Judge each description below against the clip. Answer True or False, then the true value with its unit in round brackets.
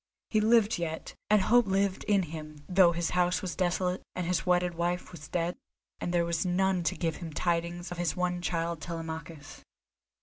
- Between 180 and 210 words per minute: True (190 wpm)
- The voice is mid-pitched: True (175 Hz)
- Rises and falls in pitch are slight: True (1.7 semitones)